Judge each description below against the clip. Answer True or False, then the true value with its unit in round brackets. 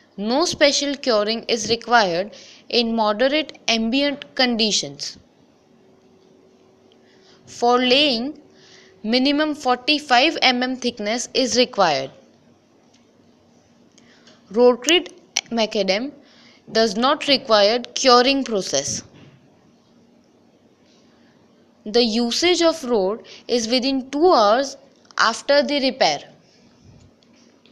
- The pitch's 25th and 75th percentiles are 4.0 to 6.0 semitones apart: False (3.6 semitones)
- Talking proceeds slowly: True (75 wpm)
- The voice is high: True (245 Hz)